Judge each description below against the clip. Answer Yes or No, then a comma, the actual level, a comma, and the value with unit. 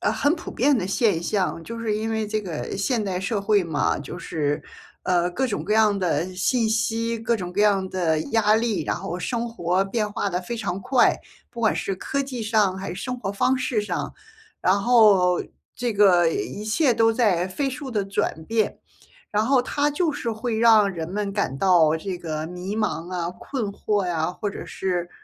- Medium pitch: No, high, 205 Hz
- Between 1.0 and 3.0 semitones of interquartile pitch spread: No, average, 4.1 semitones